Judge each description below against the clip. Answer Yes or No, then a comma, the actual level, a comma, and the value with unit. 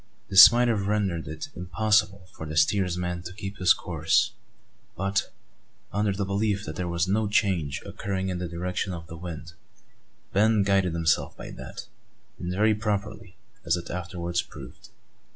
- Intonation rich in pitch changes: No, average, 2.9 semitones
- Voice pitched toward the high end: No, very low, 95 Hz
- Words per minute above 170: No, average, 160 wpm